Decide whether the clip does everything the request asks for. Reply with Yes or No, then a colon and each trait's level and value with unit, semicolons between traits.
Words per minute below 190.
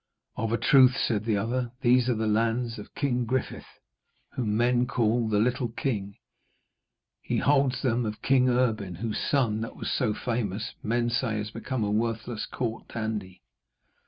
Yes: average, 165 wpm